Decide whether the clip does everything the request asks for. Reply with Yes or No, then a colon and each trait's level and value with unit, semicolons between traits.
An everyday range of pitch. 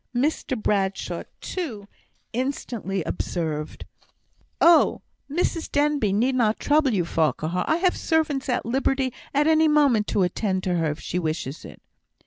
No: wide, 8.0 semitones